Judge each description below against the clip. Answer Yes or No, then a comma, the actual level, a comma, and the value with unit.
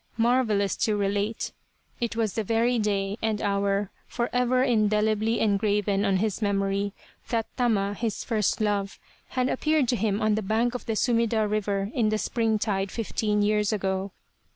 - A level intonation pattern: Yes, narrow, 2.2 semitones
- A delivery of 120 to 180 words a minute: Yes, average, 160 wpm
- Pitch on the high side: Yes, high, 215 Hz